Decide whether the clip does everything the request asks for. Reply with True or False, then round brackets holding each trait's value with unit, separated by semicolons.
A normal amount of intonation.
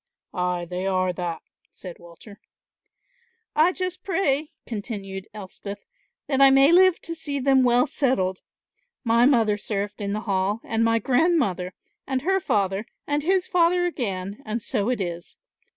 False (6.8 semitones)